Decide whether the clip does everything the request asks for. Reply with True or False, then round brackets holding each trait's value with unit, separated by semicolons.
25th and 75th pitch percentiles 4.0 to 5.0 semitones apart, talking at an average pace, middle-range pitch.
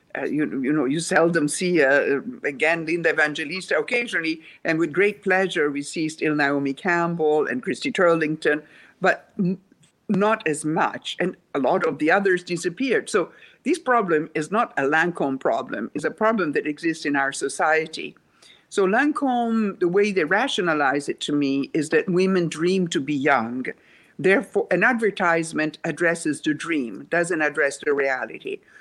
True (4.7 semitones; 160 wpm; 170 Hz)